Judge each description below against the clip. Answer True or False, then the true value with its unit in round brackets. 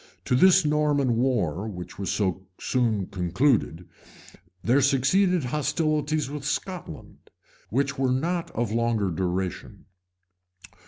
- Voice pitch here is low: True (125 Hz)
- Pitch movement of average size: False (7.1 semitones)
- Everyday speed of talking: False (110 wpm)